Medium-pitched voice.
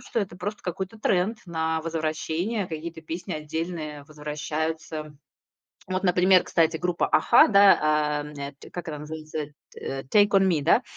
Yes: medium, 160 Hz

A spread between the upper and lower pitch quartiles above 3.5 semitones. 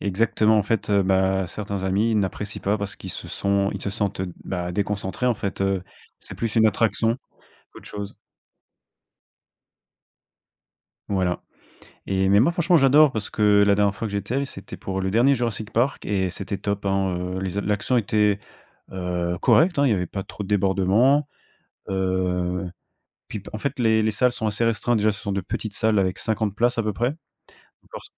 No: average, 2.8 semitones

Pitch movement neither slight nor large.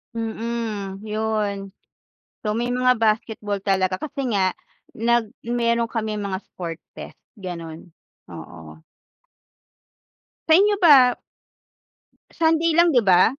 Yes: average, 3.8 semitones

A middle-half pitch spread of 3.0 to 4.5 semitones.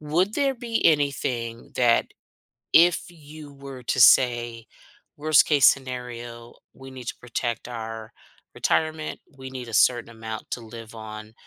Yes: average, 4.1 semitones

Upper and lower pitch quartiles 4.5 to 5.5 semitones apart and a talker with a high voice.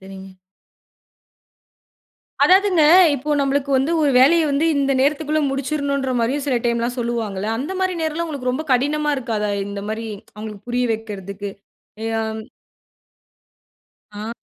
Yes: average, 5.1 semitones; very high, 260 Hz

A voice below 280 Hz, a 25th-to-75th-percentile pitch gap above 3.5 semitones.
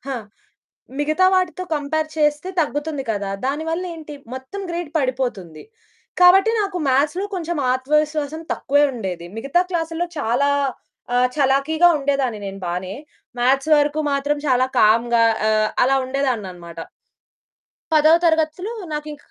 No: very high, 285 Hz; average, 4.1 semitones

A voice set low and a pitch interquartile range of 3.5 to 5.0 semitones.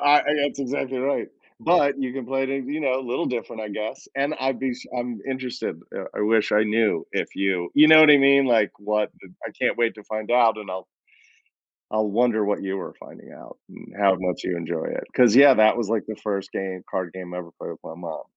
Yes: low, 115 Hz; average, 4.6 semitones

